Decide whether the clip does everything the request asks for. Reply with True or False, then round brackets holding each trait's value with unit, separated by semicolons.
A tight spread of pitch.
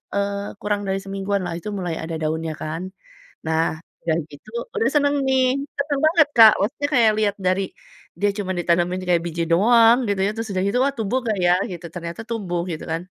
False (4.7 semitones)